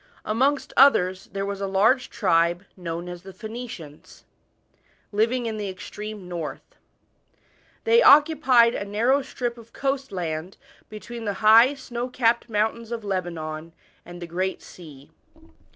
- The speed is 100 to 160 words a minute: Yes, slow, 135 wpm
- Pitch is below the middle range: No, high, 210 Hz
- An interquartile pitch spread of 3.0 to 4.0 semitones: No, average, 5.1 semitones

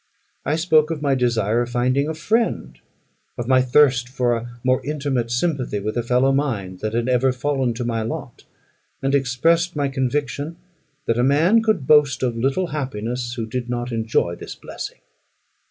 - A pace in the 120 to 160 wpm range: No, average, 175 wpm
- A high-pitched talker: No, low, 130 Hz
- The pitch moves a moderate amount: Yes, average, 3.3 semitones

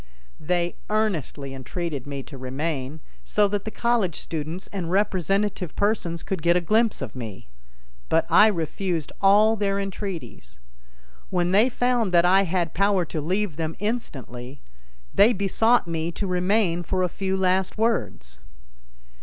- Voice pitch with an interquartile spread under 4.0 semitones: No, average, 4.4 semitones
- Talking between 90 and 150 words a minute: Yes, average, 145 wpm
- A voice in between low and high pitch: Yes, medium, 180 Hz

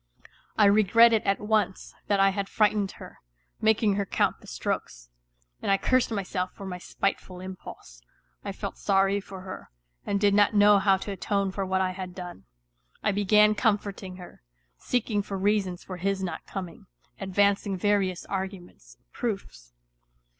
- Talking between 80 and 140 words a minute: No, average, 160 wpm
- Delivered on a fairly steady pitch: Yes, narrow, 1.7 semitones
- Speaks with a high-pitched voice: Yes, high, 195 Hz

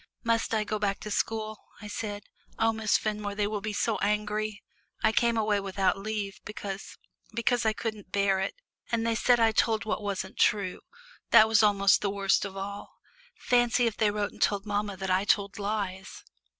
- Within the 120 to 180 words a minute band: No, average, 190 wpm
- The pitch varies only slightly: Yes, narrow, 1.6 semitones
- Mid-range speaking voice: No, high, 210 Hz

